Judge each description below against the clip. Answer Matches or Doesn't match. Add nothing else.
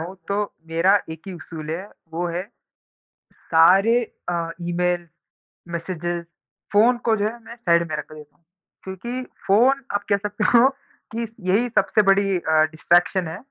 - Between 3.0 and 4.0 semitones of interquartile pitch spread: Matches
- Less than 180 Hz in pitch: Doesn't match